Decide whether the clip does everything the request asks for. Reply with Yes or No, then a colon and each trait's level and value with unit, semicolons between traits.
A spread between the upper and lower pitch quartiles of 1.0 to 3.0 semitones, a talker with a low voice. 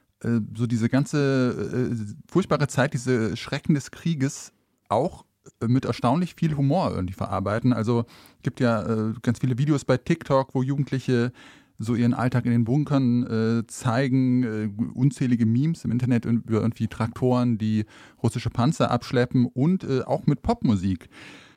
Yes: average, 2.7 semitones; low, 125 Hz